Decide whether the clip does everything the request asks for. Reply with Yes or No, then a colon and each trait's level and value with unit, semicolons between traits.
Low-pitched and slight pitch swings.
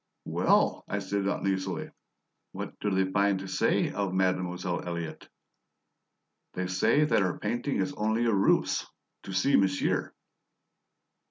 Yes: very low, 95 Hz; narrow, 1.8 semitones